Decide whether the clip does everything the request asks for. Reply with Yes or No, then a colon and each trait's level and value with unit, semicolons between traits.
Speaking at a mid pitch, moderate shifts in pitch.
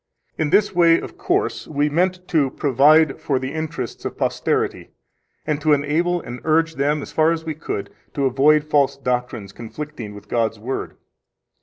Yes: medium, 150 Hz; average, 3.3 semitones